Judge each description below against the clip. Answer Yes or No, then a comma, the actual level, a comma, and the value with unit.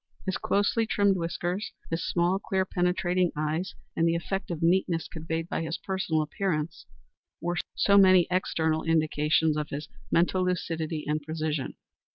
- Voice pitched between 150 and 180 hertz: Yes, medium, 170 Hz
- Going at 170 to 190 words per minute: No, average, 150 wpm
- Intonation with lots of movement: No, average, 2.8 semitones